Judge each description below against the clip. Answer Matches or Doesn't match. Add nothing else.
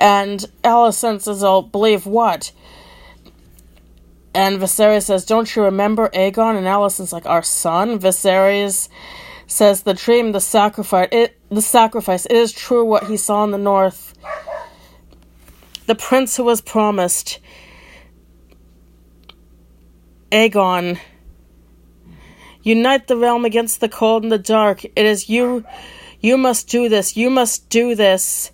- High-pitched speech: Matches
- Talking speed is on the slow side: Matches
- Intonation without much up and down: Doesn't match